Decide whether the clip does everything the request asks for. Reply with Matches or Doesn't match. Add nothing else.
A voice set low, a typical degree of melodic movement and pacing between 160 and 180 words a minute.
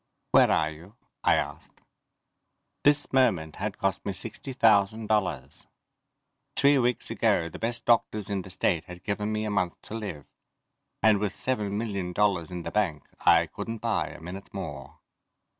Matches